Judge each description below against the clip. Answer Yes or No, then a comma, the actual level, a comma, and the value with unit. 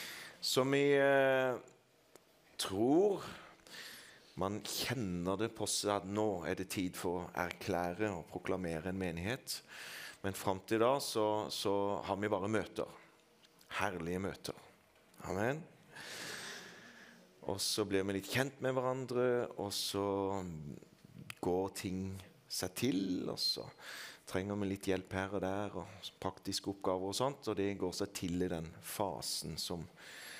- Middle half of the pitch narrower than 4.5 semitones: Yes, narrow, 2.5 semitones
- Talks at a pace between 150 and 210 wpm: No, average, 140 wpm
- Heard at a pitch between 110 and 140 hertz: No, low, 100 Hz